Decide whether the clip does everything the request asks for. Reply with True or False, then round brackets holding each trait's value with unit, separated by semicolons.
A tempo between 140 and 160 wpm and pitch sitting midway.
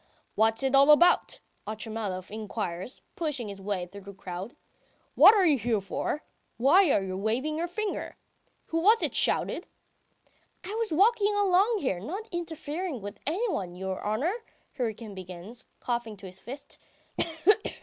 False (150 wpm; 240 Hz)